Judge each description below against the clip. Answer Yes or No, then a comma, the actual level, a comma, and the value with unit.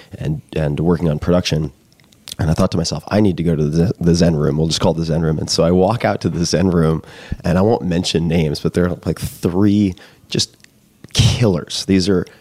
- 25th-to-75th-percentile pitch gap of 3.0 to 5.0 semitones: No, narrow, 2.5 semitones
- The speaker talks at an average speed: No, fast, 230 wpm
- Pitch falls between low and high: No, very low, 85 Hz